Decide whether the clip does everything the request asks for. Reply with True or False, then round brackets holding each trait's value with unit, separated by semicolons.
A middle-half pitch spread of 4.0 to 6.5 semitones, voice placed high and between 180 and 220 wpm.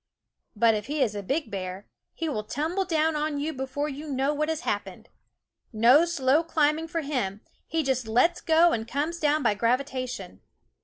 True (5.0 semitones; 285 Hz; 185 wpm)